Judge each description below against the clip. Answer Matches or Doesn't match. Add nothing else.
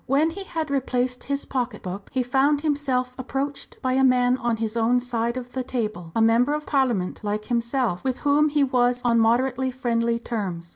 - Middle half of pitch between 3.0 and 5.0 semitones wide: Doesn't match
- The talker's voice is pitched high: Matches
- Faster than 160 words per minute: Matches